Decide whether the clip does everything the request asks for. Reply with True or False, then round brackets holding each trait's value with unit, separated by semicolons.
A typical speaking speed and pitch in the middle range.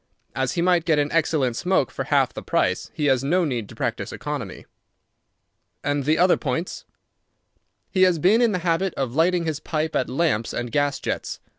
True (190 wpm; 155 Hz)